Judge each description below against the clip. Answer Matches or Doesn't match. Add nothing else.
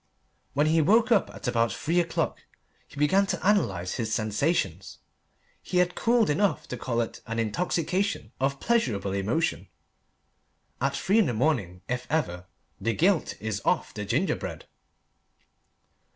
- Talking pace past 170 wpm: Doesn't match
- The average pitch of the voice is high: Doesn't match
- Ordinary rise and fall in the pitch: Doesn't match